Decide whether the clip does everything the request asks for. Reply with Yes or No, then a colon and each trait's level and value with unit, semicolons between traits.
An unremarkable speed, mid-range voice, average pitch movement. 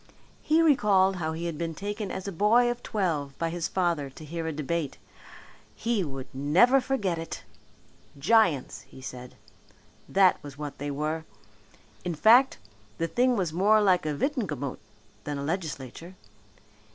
No: average, 155 wpm; medium, 170 Hz; wide, 5.8 semitones